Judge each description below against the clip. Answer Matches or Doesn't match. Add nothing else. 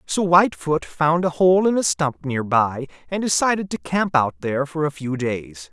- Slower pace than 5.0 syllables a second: Matches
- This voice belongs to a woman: Doesn't match